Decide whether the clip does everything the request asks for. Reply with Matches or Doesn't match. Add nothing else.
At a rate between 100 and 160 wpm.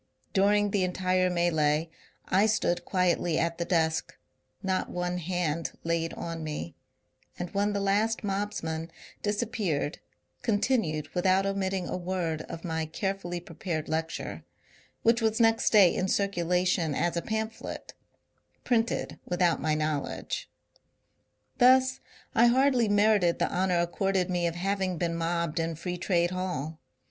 Matches